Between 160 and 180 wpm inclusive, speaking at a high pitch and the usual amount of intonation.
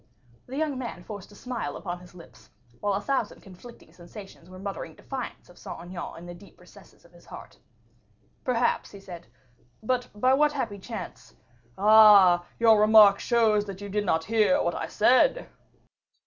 Yes: average, 175 wpm; high, 205 Hz; average, 4.7 semitones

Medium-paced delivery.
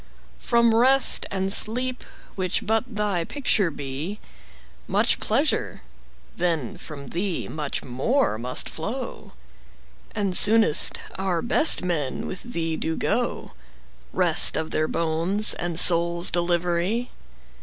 No: slow, 120 wpm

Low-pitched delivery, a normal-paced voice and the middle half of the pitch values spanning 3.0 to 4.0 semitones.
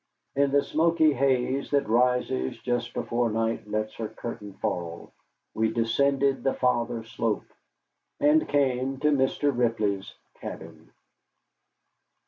No: low, 125 Hz; slow, 115 wpm; average, 3.7 semitones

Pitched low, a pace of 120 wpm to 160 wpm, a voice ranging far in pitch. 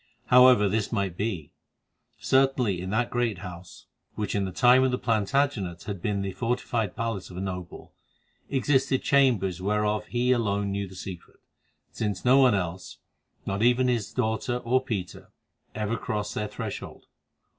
No: low, 105 Hz; average, 155 wpm; average, 4.3 semitones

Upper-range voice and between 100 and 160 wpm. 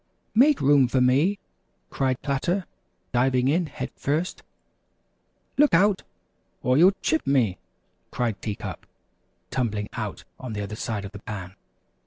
No: low, 130 Hz; average, 140 wpm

